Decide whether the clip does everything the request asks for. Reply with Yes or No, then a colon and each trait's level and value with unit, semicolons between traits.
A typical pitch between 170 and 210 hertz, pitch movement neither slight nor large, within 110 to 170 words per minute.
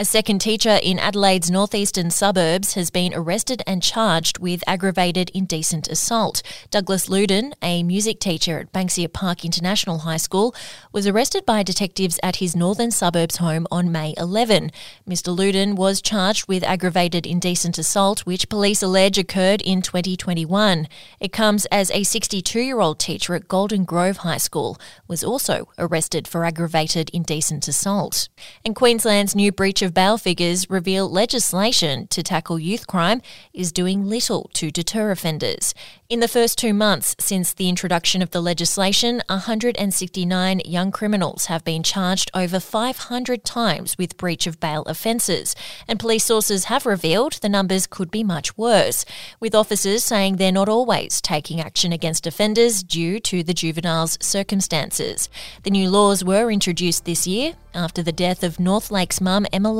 Yes: high, 190 Hz; average, 3.1 semitones; average, 155 wpm